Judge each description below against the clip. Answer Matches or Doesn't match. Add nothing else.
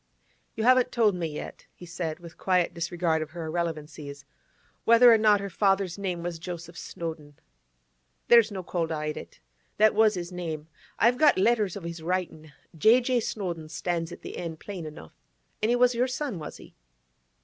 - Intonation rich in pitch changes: Doesn't match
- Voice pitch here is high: Doesn't match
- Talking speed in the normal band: Matches